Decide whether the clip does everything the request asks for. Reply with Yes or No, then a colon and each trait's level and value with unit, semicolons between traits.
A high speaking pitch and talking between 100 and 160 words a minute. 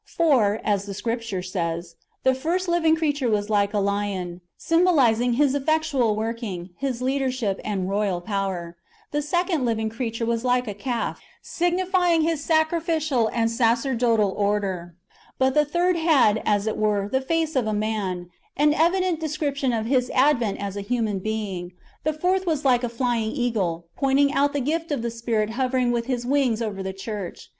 No: high, 235 Hz; average, 180 wpm